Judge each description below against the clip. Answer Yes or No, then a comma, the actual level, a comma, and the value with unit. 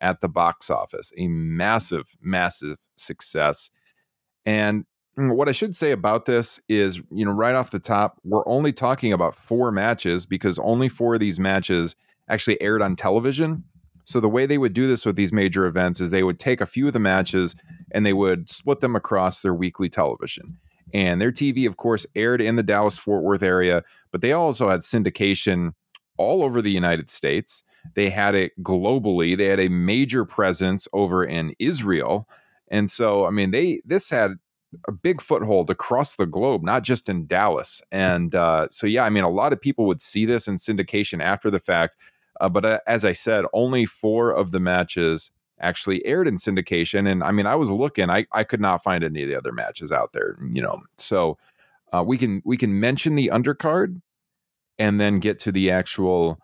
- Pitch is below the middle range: Yes, low, 100 Hz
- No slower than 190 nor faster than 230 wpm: Yes, average, 200 wpm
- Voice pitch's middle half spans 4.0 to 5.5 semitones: Yes, average, 4.3 semitones